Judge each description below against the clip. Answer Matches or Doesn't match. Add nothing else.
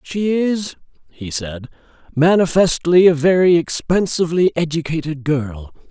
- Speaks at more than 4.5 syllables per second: Doesn't match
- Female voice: Doesn't match